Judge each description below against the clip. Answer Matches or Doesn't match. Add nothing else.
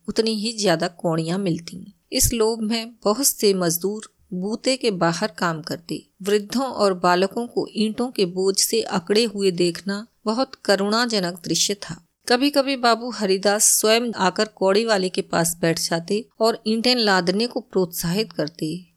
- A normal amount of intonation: Matches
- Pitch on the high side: Matches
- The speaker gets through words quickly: Doesn't match